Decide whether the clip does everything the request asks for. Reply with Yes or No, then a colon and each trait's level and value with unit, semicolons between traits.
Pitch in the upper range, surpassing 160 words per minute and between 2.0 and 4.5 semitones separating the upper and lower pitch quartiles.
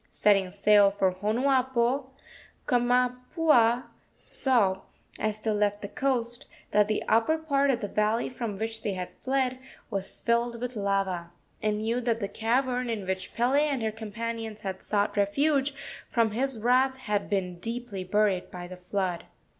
No: high, 225 Hz; average, 155 wpm; average, 3.7 semitones